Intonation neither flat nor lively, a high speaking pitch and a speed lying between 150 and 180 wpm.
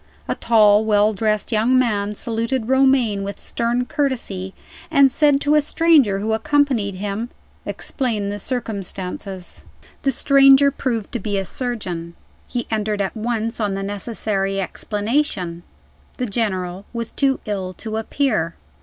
No: average, 4.2 semitones; high, 220 Hz; average, 140 wpm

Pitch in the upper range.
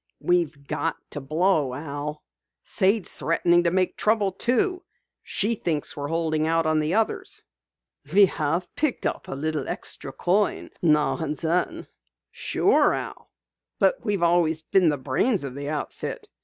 No: medium, 165 Hz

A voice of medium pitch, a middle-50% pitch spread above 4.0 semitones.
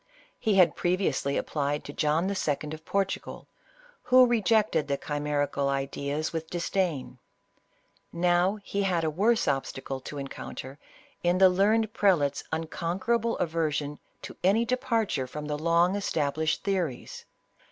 Yes: medium, 165 Hz; average, 5.0 semitones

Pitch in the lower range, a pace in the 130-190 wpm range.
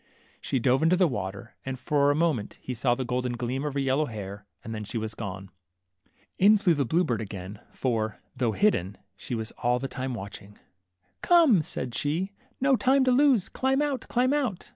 No: low, 130 Hz; average, 200 wpm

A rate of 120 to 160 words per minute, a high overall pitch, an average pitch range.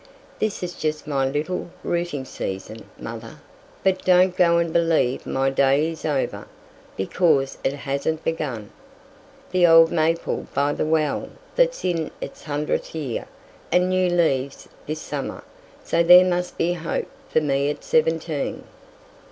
No: average, 145 wpm; medium, 160 Hz; average, 3.9 semitones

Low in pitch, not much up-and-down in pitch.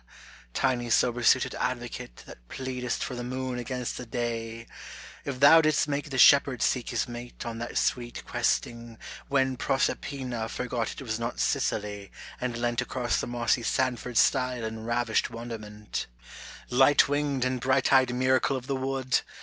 Yes: low, 125 Hz; narrow, 1.9 semitones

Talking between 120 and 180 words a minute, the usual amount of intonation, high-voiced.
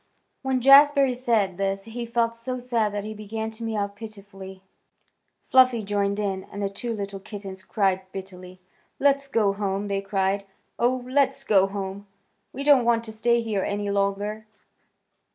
Yes: average, 160 wpm; average, 3.1 semitones; high, 210 Hz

